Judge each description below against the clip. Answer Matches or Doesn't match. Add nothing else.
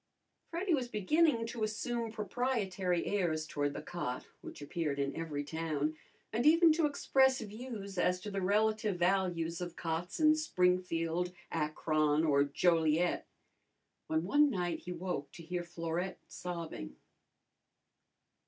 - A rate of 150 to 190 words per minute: Doesn't match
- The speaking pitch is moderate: Matches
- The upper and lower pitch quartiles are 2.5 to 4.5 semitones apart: Doesn't match